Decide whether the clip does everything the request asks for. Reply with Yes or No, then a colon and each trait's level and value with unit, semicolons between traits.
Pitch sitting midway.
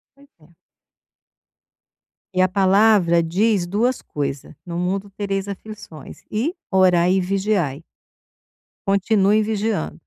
No: high, 195 Hz